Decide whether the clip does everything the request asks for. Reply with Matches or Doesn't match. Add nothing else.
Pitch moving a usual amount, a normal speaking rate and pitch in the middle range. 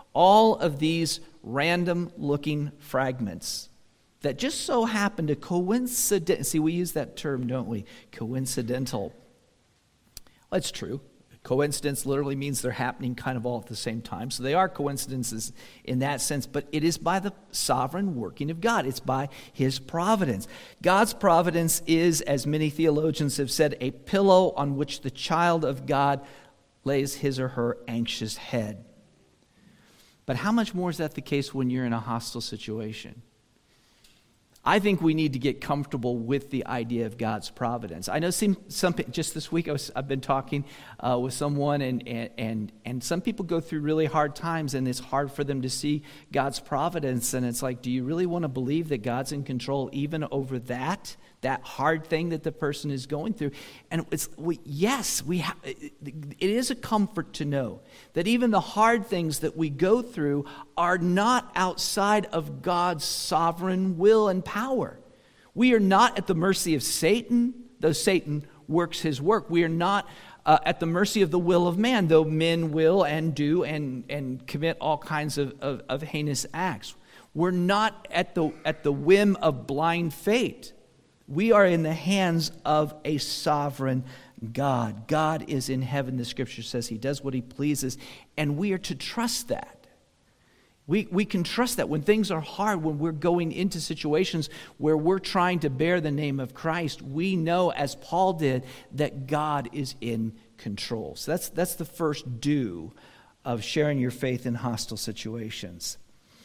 Matches